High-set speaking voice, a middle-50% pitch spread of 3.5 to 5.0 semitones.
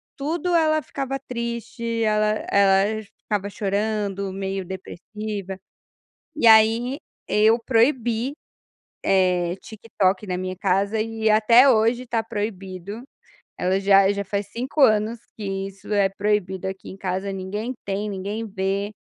No: high, 210 Hz; average, 2.8 semitones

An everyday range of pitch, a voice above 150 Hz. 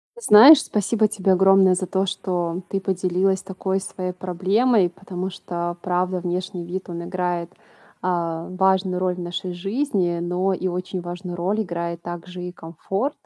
No: narrow, 1.5 semitones; medium, 185 Hz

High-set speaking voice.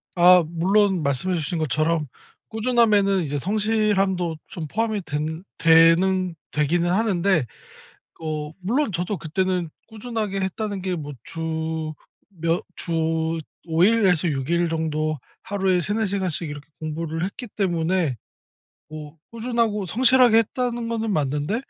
No: medium, 180 Hz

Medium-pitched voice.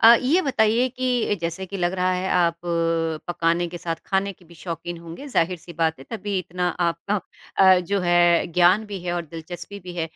Yes: medium, 180 Hz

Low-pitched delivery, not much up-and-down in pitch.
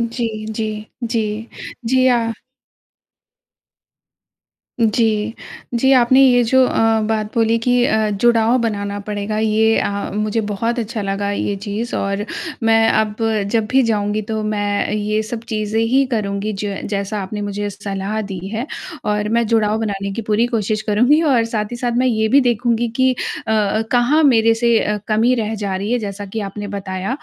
No: high, 220 Hz; narrow, 2.2 semitones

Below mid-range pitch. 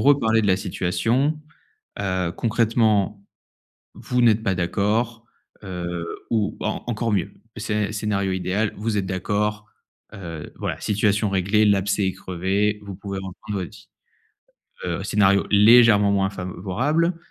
Yes: low, 105 Hz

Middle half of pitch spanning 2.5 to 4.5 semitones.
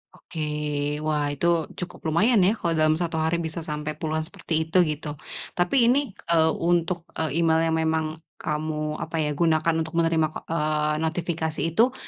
No: narrow, 1.4 semitones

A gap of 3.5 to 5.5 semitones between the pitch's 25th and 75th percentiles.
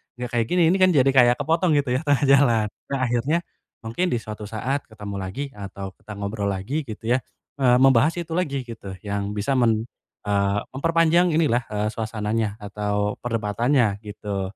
Yes: average, 5.0 semitones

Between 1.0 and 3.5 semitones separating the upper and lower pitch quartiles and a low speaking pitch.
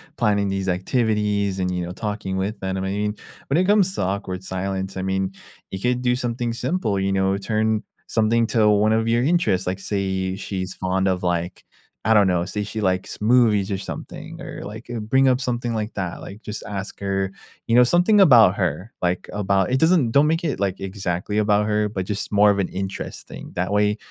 Yes: average, 3.2 semitones; low, 105 Hz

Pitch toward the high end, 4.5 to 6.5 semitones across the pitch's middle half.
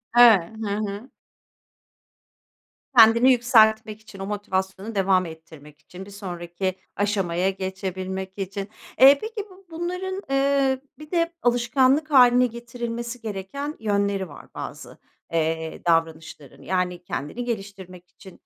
Yes: high, 205 Hz; average, 4.8 semitones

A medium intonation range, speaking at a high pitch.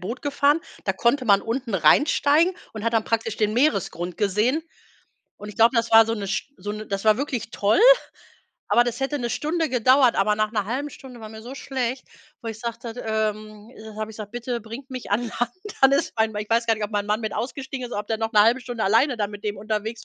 Yes: average, 3.0 semitones; high, 225 Hz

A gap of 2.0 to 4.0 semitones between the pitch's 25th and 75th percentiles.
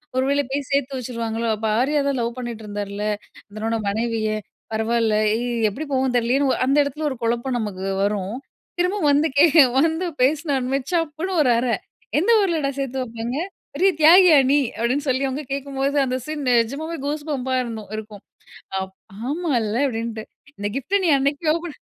No: average, 4.4 semitones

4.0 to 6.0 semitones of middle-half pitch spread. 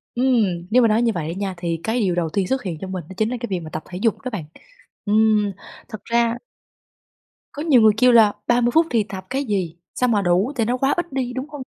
Yes: average, 4.7 semitones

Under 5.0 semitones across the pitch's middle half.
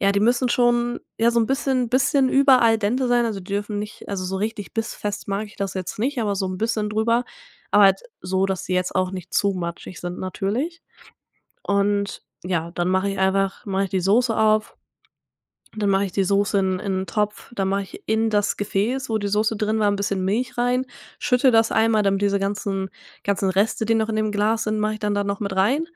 Yes: narrow, 2.6 semitones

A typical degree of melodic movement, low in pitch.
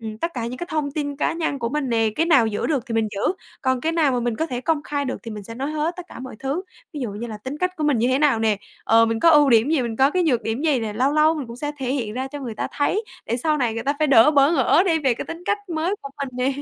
No: average, 4.7 semitones; very high, 270 Hz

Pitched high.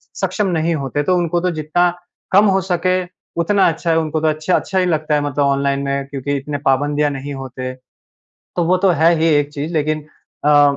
No: medium, 155 Hz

